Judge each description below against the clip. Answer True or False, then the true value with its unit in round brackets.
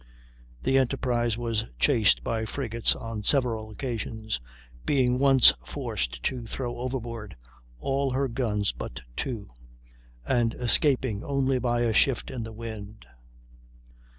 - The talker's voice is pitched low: True (120 Hz)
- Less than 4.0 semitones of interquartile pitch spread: True (2.9 semitones)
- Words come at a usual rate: False (125 wpm)